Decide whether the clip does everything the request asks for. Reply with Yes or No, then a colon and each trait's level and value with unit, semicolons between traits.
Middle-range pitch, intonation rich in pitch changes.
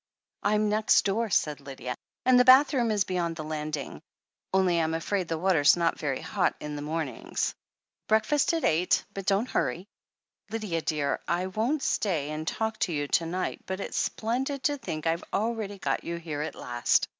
Yes: medium, 180 Hz; wide, 5.7 semitones